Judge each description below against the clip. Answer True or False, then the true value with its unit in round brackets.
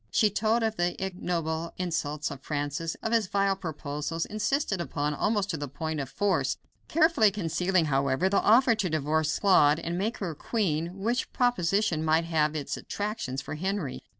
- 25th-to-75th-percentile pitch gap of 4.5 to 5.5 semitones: True (5.1 semitones)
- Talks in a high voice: False (170 Hz)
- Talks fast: False (175 wpm)